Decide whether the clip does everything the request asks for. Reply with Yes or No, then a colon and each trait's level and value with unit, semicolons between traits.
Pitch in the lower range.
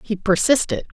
No: high, 200 Hz